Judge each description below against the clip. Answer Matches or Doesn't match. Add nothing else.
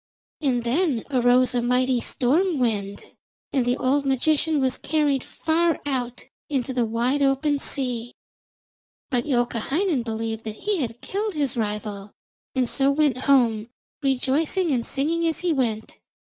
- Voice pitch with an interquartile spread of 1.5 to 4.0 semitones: Matches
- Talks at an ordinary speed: Matches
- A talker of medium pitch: Doesn't match